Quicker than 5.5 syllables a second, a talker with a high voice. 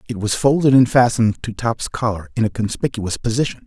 No: 5.8 syllables/s; low, 115 Hz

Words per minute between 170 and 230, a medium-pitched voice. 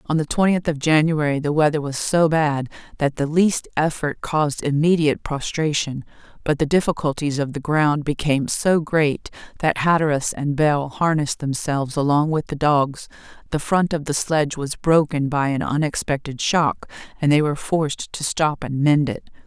Yes: average, 175 wpm; medium, 150 Hz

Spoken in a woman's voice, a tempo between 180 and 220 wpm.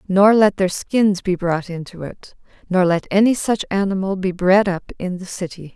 Yes: female; average, 200 wpm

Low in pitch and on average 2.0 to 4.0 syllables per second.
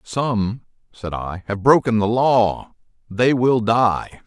Yes: low, 110 Hz; 3.1 syllables/s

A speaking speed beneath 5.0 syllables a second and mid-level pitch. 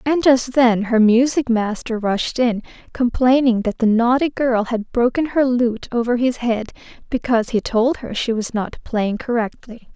No: 4.5 syllables/s; high, 240 Hz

